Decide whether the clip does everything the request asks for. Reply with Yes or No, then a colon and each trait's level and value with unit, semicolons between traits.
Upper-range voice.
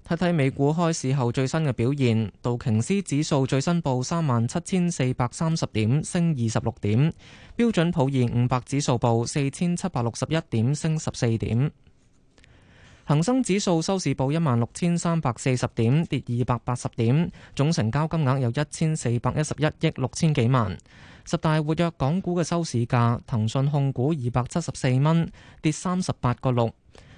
No: low, 135 Hz